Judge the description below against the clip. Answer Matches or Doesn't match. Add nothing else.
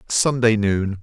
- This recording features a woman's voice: Doesn't match